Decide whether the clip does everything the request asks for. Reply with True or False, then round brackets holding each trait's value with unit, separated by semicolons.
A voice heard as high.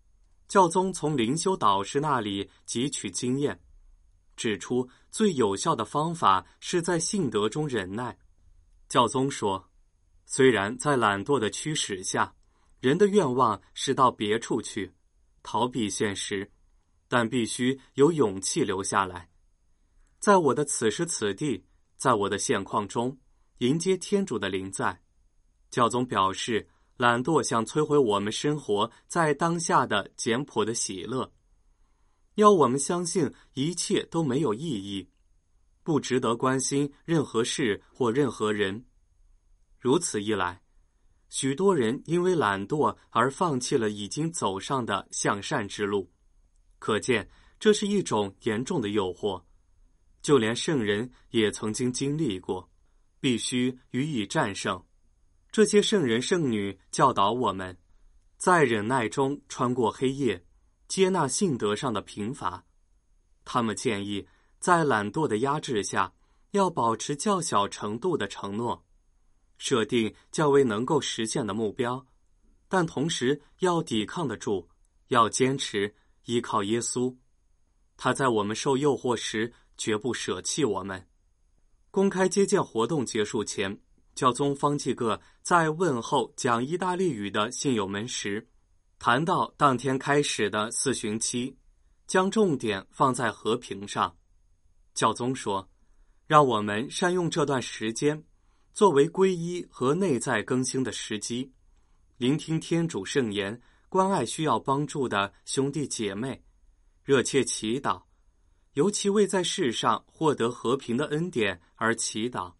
False (115 Hz)